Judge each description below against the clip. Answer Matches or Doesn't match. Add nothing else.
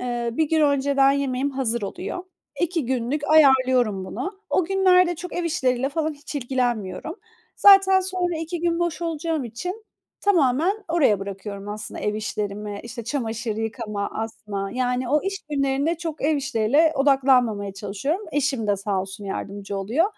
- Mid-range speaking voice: Doesn't match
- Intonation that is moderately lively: Doesn't match